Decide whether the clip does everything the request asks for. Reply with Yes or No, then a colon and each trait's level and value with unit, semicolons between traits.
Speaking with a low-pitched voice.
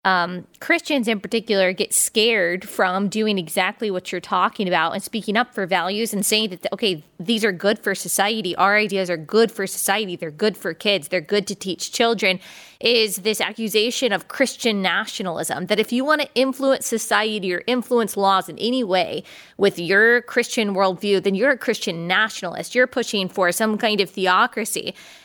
No: high, 205 Hz